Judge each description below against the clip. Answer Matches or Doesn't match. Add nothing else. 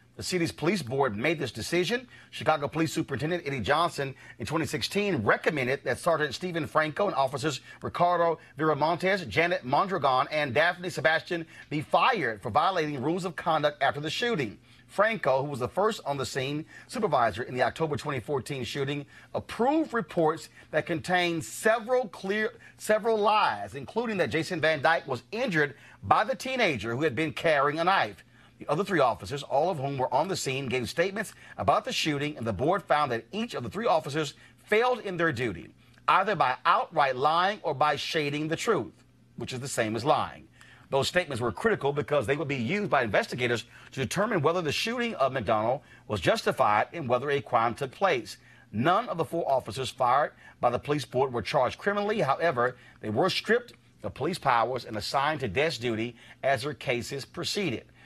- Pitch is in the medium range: Matches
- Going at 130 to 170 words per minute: Doesn't match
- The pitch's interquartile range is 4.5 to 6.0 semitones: Matches